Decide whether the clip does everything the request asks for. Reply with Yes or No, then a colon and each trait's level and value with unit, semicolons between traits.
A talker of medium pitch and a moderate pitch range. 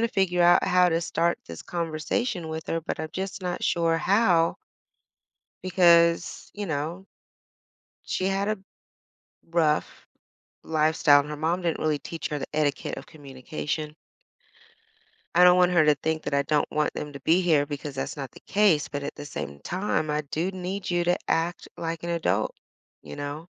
Yes: medium, 165 Hz; average, 3.0 semitones